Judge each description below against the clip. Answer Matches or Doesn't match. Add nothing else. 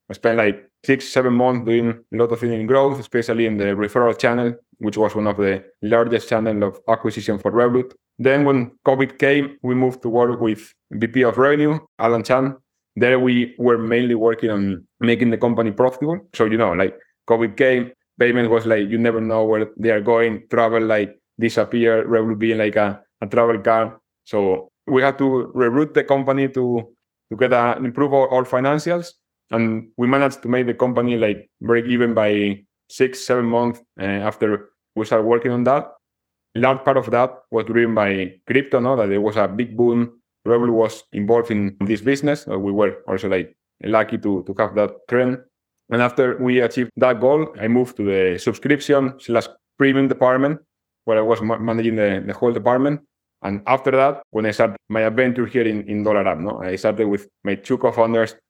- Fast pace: Doesn't match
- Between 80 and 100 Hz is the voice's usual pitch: Doesn't match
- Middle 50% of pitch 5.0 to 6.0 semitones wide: Doesn't match